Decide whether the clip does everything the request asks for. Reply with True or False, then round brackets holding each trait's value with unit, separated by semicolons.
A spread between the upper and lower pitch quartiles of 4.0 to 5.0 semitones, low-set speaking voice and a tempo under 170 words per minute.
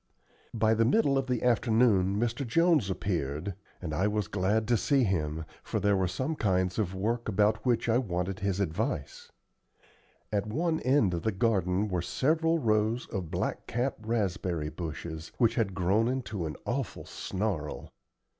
True (4.5 semitones; 105 Hz; 160 wpm)